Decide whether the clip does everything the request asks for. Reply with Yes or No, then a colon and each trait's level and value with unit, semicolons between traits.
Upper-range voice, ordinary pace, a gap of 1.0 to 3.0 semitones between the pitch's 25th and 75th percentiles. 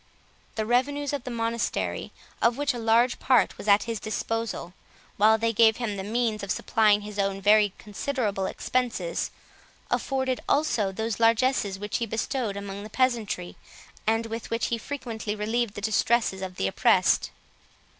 Yes: high, 225 Hz; average, 160 wpm; average, 2.7 semitones